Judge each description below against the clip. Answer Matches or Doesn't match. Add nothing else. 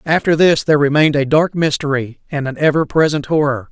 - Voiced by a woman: Doesn't match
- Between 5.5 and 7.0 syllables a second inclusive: Matches